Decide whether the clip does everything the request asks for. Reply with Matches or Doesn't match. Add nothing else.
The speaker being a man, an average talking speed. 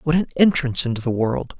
Doesn't match